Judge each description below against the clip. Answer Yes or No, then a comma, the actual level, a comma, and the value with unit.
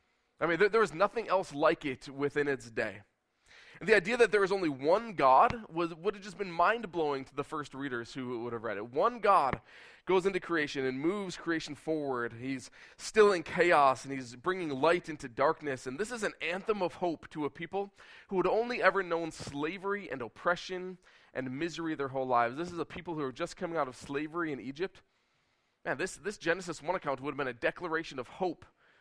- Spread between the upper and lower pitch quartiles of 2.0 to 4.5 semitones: No, average, 5.2 semitones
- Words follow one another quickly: Yes, fast, 215 wpm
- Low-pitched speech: No, medium, 165 Hz